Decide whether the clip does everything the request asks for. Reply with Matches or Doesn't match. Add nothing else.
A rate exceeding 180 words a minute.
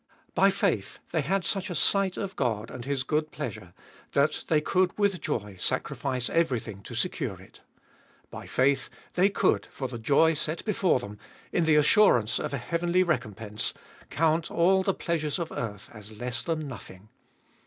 Doesn't match